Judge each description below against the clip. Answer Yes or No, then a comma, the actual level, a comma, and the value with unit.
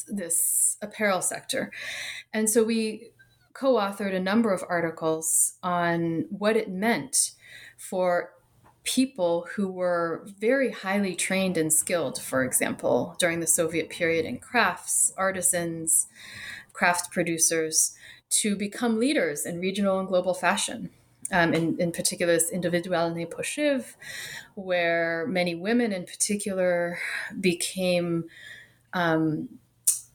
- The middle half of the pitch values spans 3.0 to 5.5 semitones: Yes, average, 3.6 semitones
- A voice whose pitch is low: No, medium, 180 Hz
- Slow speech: Yes, slow, 115 wpm